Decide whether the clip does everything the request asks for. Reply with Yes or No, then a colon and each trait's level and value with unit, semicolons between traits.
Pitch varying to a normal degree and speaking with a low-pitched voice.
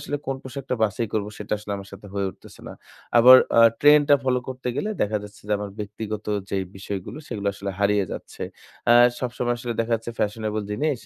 Yes: average, 3.6 semitones; low, 110 Hz